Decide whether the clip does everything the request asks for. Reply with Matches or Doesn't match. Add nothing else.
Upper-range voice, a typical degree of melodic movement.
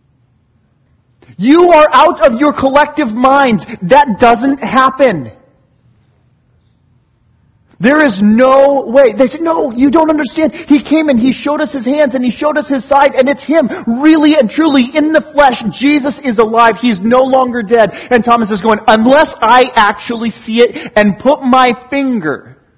Matches